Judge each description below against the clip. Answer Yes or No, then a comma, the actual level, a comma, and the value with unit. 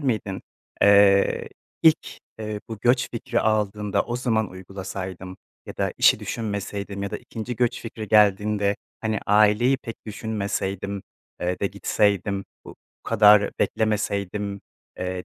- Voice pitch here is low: Yes, low, 105 Hz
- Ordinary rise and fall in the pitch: No, narrow, 1.8 semitones